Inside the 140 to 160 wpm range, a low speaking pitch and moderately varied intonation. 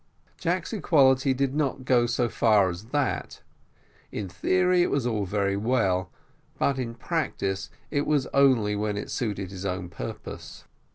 No: average, 155 wpm; low, 120 Hz; wide, 5.8 semitones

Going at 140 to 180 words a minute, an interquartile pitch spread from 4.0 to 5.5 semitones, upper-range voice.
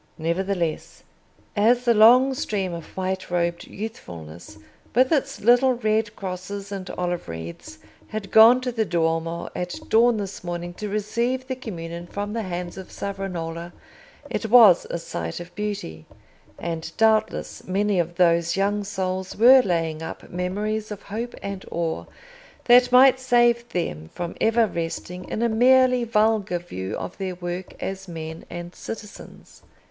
Yes: average, 150 wpm; average, 4.5 semitones; high, 195 Hz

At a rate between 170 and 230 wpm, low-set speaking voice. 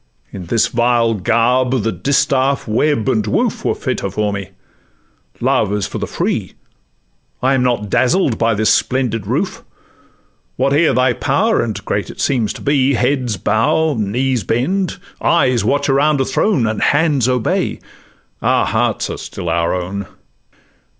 No: average, 150 wpm; low, 125 Hz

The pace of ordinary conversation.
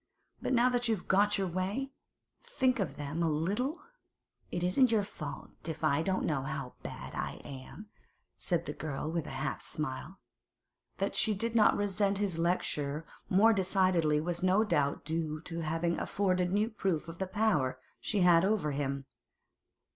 Yes: average, 170 wpm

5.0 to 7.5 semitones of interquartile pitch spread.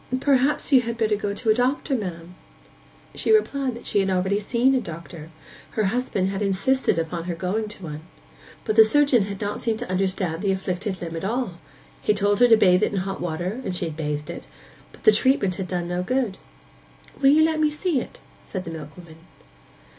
Yes: wide, 5.4 semitones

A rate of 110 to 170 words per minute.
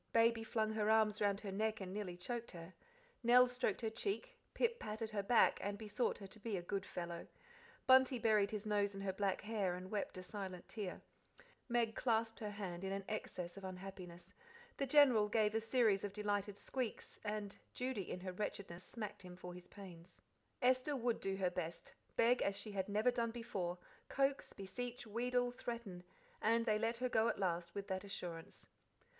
No: average, 190 wpm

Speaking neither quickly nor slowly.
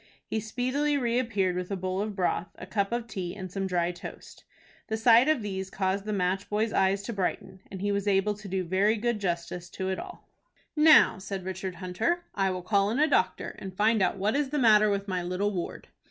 No: fast, 220 wpm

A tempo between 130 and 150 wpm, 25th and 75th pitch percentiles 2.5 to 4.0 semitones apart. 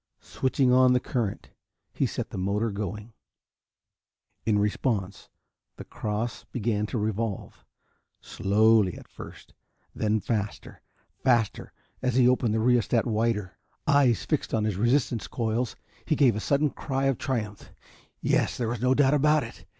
Yes: average, 145 wpm; average, 3.3 semitones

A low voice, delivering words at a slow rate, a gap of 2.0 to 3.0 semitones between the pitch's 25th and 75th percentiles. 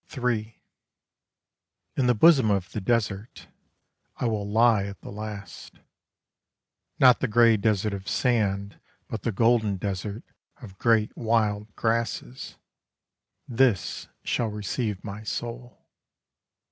Yes: low, 110 Hz; slow, 115 wpm; narrow, 2.6 semitones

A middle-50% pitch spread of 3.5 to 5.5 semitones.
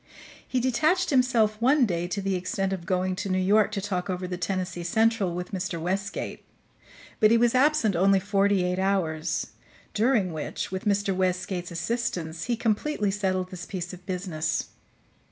No: average, 3.1 semitones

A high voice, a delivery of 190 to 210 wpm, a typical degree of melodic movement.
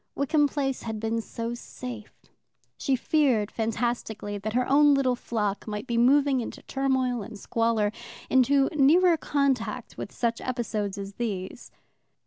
No: high, 240 Hz; average, 140 wpm; average, 3.8 semitones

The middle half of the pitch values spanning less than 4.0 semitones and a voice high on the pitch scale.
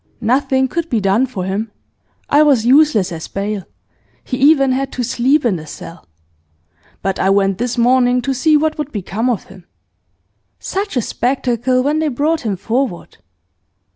No: average, 5.2 semitones; high, 245 Hz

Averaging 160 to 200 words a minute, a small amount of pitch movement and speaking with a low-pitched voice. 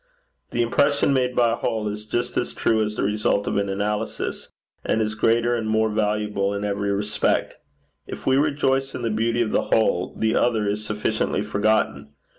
Yes: average, 190 wpm; narrow, 2.1 semitones; low, 110 Hz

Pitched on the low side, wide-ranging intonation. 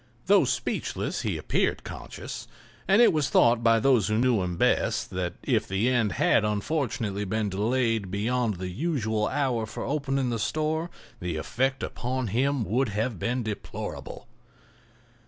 No: low, 115 Hz; average, 4.3 semitones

